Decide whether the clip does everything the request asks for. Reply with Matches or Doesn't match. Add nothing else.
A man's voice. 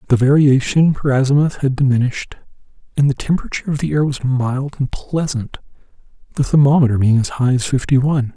Matches